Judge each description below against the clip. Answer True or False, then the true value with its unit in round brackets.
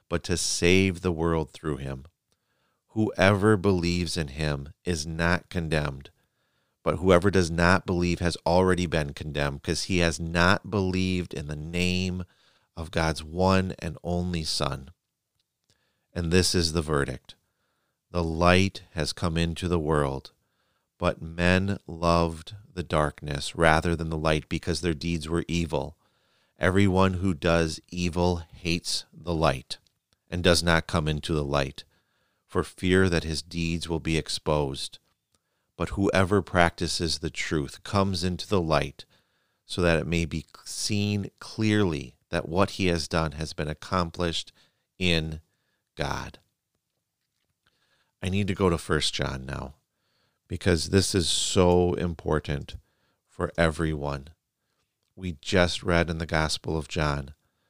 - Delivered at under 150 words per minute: True (140 wpm)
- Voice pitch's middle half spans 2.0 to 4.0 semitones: True (2.6 semitones)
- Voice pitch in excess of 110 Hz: False (85 Hz)